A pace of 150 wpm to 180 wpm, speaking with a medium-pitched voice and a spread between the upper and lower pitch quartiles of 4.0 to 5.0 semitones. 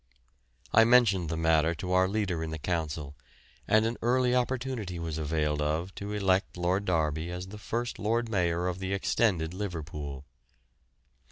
No: average, 160 wpm; very low, 90 Hz; average, 4.7 semitones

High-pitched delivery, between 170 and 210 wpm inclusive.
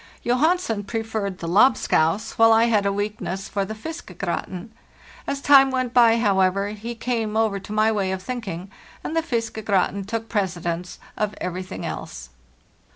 No: high, 215 Hz; average, 155 wpm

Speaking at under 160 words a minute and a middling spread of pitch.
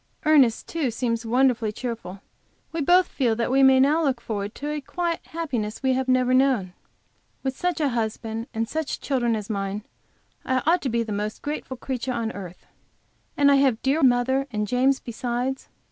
No: average, 190 wpm; average, 3.4 semitones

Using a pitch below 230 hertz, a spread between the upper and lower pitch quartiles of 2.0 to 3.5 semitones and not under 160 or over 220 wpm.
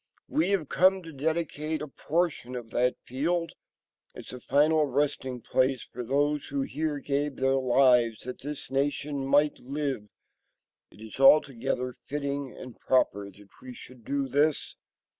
No: medium, 140 Hz; average, 2.8 semitones; average, 150 wpm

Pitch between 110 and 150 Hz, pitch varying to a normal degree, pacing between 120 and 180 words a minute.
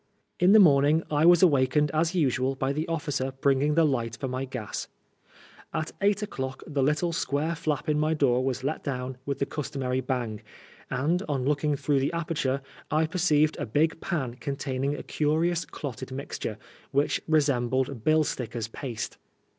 Yes: medium, 140 Hz; average, 3.1 semitones; average, 175 wpm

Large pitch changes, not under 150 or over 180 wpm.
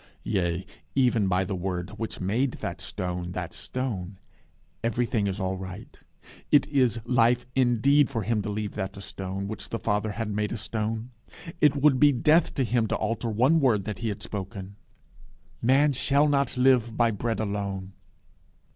No: average, 4.3 semitones; average, 175 wpm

